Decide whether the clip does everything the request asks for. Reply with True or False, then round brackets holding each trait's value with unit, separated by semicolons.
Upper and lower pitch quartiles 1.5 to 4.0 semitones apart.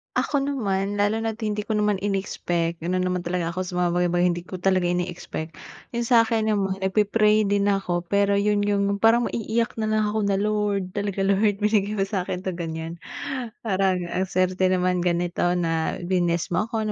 True (2.8 semitones)